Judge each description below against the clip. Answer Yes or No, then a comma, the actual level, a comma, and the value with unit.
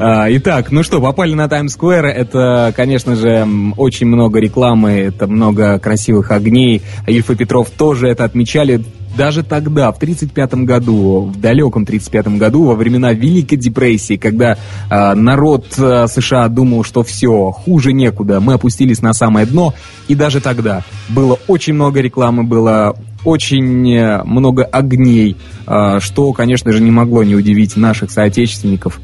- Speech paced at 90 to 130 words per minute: No, average, 140 wpm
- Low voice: Yes, low, 120 Hz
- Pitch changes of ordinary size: Yes, average, 3.6 semitones